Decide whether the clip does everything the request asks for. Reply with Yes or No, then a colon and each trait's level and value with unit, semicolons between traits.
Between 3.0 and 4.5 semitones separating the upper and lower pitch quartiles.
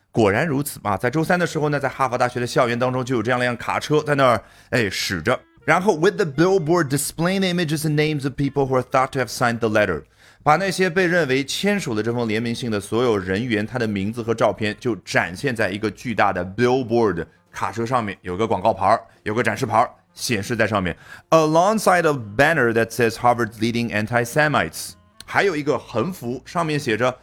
No: average, 4.9 semitones